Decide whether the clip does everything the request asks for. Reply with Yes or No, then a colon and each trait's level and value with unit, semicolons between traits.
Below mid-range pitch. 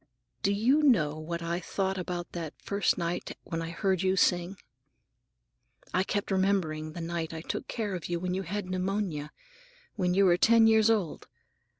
No: medium, 185 Hz